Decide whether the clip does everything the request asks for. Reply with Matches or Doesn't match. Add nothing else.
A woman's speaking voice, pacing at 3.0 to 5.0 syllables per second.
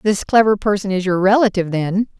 Doesn't match